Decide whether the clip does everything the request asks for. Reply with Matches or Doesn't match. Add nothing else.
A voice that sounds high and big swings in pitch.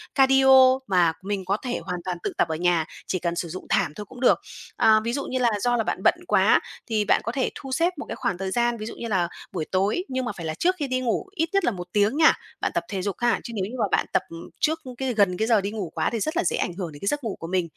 Matches